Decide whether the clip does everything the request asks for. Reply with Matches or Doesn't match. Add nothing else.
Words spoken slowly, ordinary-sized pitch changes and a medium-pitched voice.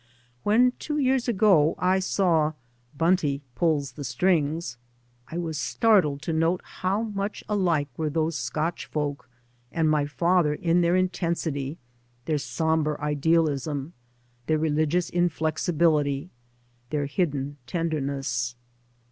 Matches